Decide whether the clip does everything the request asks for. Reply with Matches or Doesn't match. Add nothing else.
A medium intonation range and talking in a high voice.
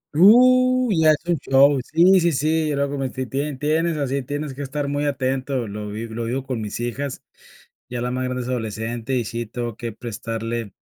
Doesn't match